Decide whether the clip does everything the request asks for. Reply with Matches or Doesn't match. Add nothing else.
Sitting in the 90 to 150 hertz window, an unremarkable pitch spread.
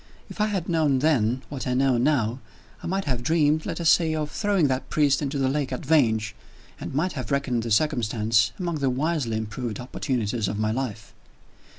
Matches